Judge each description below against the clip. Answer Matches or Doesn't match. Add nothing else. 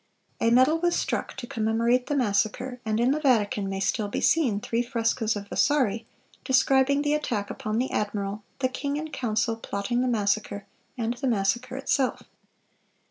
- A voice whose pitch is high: Matches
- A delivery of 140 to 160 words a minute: Doesn't match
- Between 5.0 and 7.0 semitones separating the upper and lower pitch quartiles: Doesn't match